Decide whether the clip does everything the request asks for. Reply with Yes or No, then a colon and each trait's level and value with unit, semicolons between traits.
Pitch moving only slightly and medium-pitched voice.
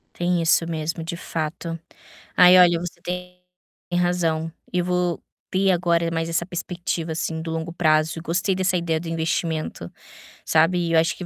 Yes: narrow, 1.5 semitones; medium, 170 Hz